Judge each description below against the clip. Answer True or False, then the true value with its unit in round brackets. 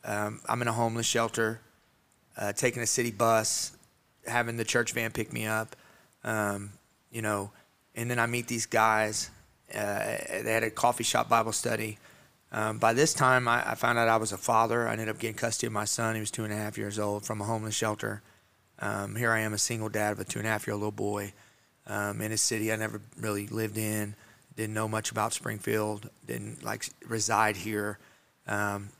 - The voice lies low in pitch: True (110 Hz)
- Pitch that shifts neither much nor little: False (1.6 semitones)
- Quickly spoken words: True (215 wpm)